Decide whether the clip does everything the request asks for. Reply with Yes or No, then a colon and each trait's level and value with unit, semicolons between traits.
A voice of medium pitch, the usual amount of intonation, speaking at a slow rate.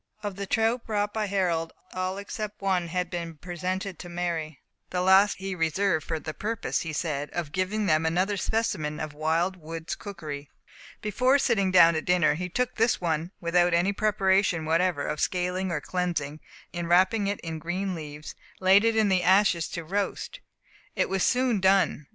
No: medium, 180 Hz; average, 3.4 semitones; average, 185 wpm